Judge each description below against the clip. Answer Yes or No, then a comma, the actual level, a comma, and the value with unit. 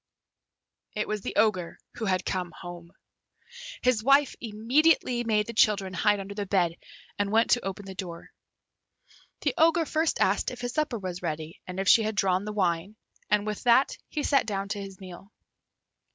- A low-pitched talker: No, high, 205 Hz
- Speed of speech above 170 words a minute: Yes, average, 180 wpm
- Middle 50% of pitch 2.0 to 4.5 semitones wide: Yes, average, 3.8 semitones